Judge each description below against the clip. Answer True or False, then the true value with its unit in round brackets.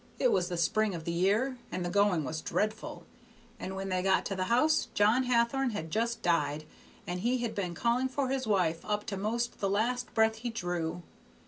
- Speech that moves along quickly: True (210 wpm)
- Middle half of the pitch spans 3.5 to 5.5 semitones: True (4.8 semitones)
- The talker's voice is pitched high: True (210 Hz)